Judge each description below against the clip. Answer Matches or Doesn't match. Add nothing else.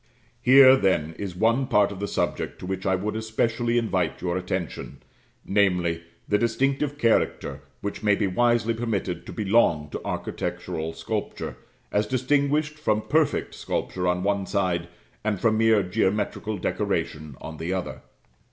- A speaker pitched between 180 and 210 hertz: Doesn't match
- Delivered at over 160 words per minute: Doesn't match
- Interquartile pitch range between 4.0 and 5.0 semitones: Matches